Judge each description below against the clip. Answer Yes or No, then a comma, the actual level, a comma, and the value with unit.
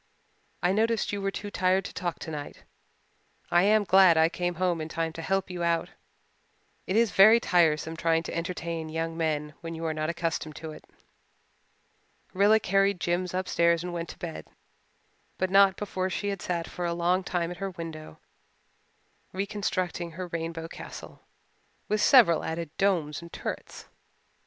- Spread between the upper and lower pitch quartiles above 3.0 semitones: No, average, 2.7 semitones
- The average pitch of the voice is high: No, medium, 175 Hz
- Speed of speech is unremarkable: Yes, average, 165 wpm